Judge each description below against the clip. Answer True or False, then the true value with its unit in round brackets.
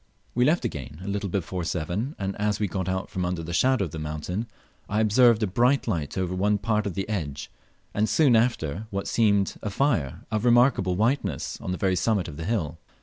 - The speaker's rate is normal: False (210 wpm)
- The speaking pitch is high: False (100 Hz)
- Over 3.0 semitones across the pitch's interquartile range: True (4.2 semitones)